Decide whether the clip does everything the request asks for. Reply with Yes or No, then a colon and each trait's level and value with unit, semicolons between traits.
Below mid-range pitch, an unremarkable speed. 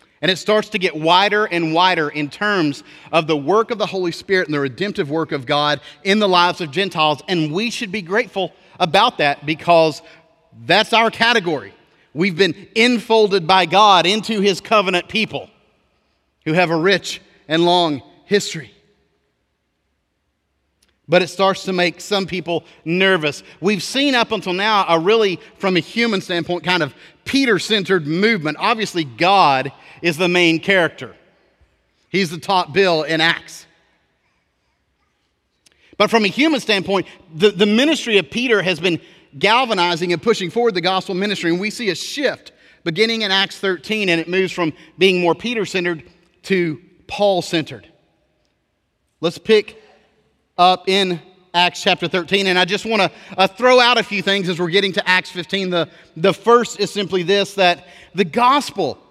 No: medium, 185 Hz; average, 165 wpm